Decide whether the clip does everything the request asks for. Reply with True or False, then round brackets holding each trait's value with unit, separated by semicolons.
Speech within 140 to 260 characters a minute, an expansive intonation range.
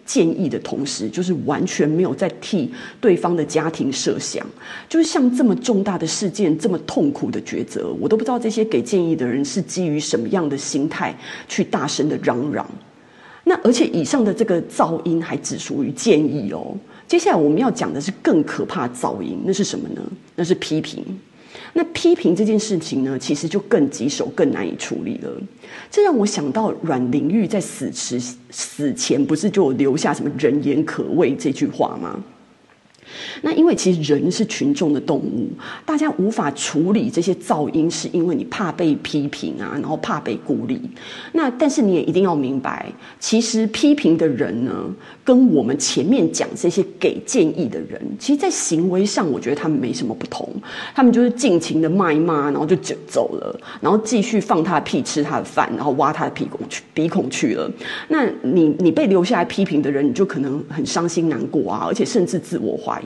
False (290 characters per minute; 7.1 semitones)